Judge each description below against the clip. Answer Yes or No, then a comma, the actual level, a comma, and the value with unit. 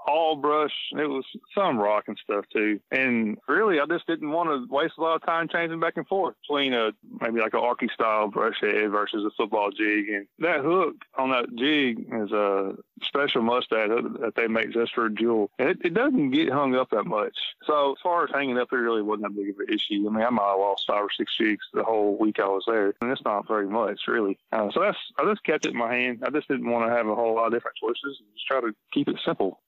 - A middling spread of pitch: No, wide, 7.0 semitones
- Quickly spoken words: Yes, fast, 255 wpm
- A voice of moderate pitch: No, low, 125 Hz